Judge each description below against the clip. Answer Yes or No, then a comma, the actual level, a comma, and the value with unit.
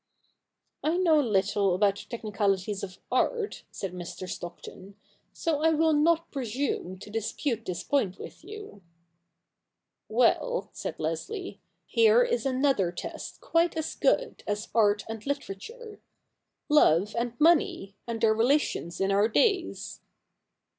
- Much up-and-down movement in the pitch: Yes, wide, 8.3 semitones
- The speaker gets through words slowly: No, average, 145 wpm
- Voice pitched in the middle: No, high, 230 Hz